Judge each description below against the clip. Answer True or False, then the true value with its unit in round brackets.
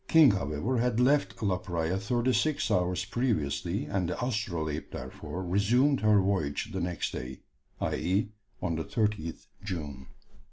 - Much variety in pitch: True (6.0 semitones)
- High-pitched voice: False (95 Hz)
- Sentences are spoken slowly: False (145 wpm)